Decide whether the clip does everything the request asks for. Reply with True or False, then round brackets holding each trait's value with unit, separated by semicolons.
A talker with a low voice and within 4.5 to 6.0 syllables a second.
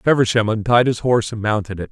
False (110 Hz; 6.4 syllables/s)